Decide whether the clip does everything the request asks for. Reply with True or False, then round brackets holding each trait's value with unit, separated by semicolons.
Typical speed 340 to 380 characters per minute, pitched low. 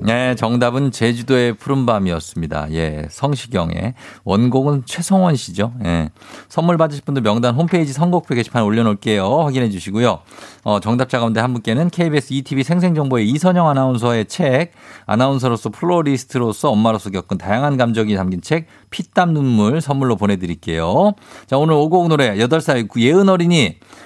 True (370 characters per minute; 125 Hz)